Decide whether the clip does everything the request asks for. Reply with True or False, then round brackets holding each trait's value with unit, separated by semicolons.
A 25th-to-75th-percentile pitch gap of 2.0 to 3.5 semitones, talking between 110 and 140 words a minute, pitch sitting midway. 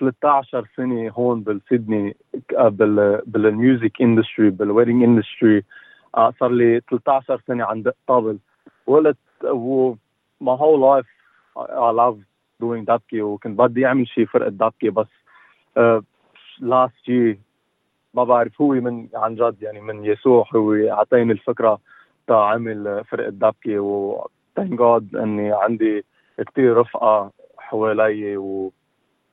False (2.6 semitones; 120 wpm; 115 Hz)